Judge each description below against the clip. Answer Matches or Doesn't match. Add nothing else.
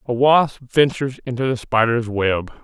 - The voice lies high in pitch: Doesn't match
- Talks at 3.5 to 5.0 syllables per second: Matches